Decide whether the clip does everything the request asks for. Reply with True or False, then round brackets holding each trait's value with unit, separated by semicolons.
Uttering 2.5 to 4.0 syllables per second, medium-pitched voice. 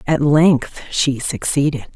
True (3.5 syllables/s; 145 Hz)